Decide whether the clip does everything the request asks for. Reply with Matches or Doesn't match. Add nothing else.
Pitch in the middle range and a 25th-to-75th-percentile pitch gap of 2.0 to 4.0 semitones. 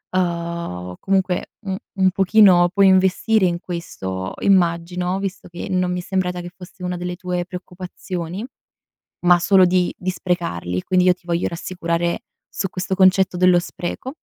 Doesn't match